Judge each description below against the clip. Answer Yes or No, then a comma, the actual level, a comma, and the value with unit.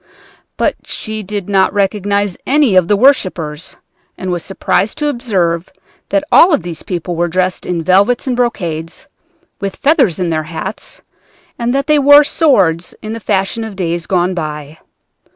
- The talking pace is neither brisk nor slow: Yes, average, 165 wpm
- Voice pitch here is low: No, high, 195 Hz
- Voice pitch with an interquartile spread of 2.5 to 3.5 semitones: No, average, 5.3 semitones